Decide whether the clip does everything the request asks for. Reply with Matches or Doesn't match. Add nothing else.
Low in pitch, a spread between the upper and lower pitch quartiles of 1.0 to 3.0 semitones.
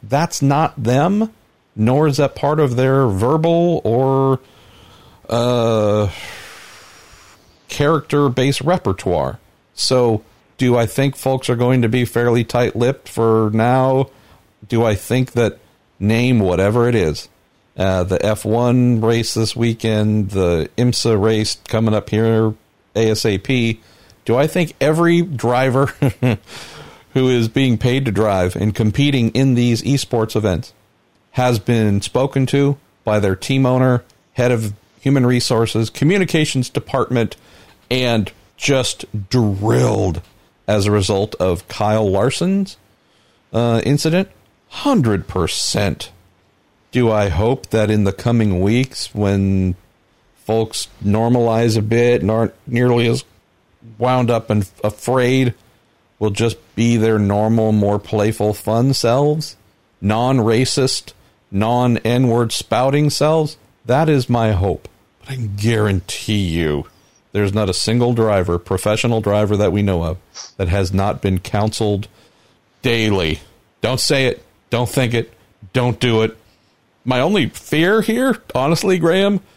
Doesn't match